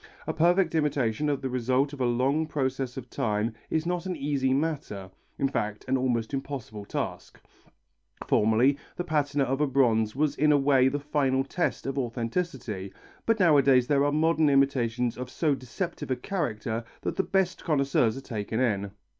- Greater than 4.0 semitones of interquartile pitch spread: No, average, 3.6 semitones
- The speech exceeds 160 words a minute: Yes, average, 175 wpm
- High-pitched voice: No, low, 135 Hz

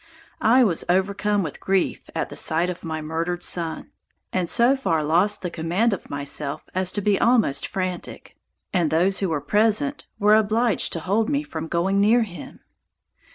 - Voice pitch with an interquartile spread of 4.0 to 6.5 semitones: Yes, average, 4.3 semitones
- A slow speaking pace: No, average, 175 wpm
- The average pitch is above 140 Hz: Yes, medium, 185 Hz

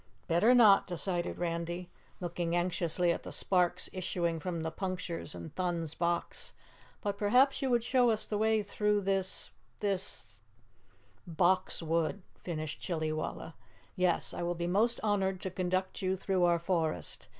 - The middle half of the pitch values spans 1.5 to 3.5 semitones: Yes, average, 2.7 semitones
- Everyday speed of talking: Yes, average, 150 wpm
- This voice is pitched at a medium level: Yes, medium, 180 Hz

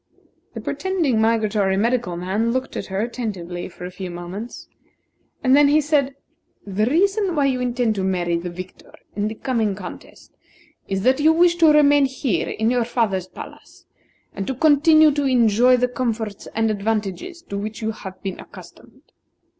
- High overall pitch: Yes, high, 230 Hz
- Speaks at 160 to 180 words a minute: Yes, average, 170 wpm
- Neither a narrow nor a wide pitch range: No, wide, 6.0 semitones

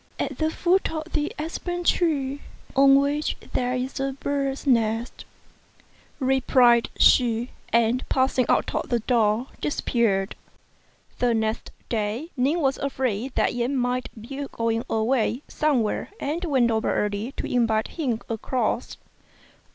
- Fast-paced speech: No, slow, 135 wpm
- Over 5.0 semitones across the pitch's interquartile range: No, average, 3.5 semitones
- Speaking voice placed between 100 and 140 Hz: No, very high, 255 Hz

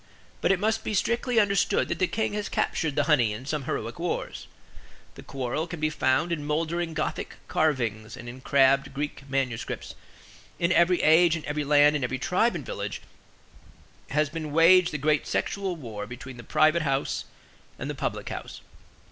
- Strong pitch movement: No, average, 4.2 semitones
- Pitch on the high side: No, medium, 150 Hz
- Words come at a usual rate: Yes, average, 180 wpm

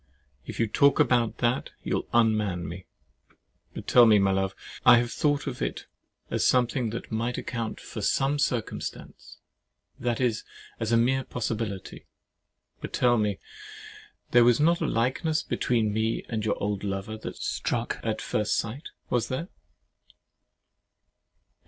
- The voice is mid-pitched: No, low, 115 Hz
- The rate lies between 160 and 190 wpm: No, average, 145 wpm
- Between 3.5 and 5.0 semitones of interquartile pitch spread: No, average, 2.7 semitones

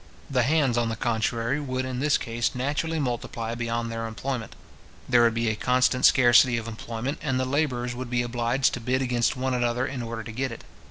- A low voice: Yes, low, 120 Hz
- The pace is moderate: No, fast, 210 wpm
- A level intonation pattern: Yes, narrow, 1.9 semitones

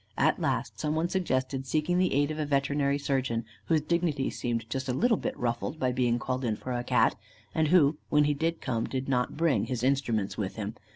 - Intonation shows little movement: No, average, 3.8 semitones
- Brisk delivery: Yes, fast, 220 wpm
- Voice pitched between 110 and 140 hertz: Yes, low, 135 Hz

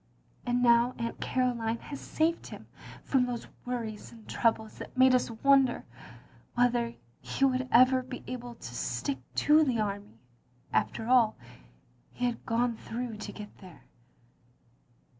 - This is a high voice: Yes, high, 240 Hz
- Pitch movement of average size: No, narrow, 2.3 semitones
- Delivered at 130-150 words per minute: Yes, average, 140 wpm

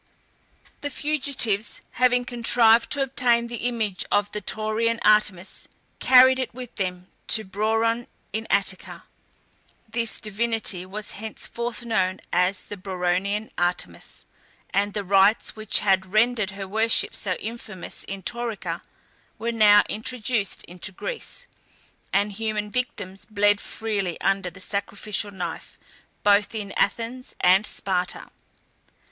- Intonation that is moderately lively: Yes, average, 3.0 semitones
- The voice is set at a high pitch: Yes, high, 210 Hz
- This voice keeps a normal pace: No, slow, 125 wpm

